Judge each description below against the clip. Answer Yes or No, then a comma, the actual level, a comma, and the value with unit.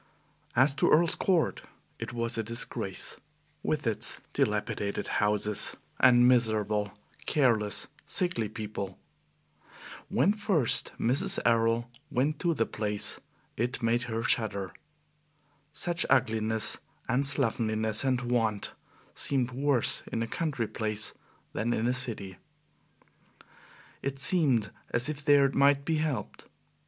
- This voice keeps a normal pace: No, slow, 120 wpm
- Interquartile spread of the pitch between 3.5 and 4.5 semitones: Yes, average, 4.1 semitones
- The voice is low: Yes, low, 120 Hz